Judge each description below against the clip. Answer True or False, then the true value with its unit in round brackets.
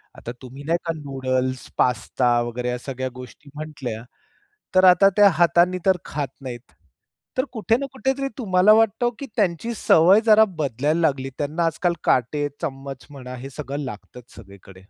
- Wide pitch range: True (6.1 semitones)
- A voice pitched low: False (145 Hz)